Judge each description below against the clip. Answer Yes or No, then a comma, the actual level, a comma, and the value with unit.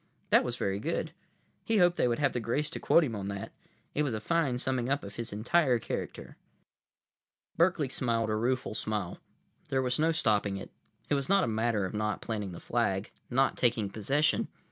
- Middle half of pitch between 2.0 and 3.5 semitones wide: No, average, 4.8 semitones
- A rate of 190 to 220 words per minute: Yes, average, 200 wpm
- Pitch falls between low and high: No, low, 120 Hz